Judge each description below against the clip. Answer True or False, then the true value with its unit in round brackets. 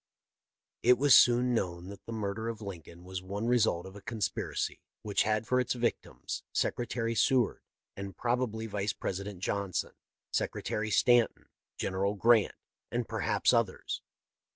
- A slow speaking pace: False (150 wpm)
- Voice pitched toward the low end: True (110 Hz)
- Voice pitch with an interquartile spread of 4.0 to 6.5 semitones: False (3.2 semitones)